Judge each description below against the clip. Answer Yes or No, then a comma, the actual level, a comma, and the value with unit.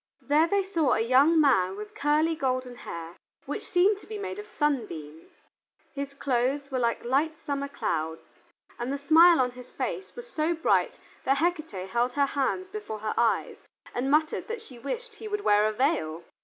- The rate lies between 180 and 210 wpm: Yes, average, 185 wpm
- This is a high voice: Yes, very high, 280 Hz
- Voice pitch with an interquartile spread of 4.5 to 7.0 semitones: Yes, wide, 5.6 semitones